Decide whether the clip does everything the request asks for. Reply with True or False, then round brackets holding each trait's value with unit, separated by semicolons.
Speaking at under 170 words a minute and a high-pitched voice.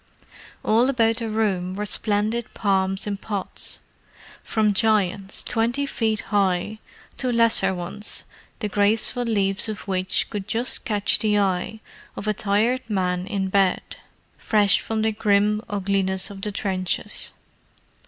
True (135 wpm; 205 Hz)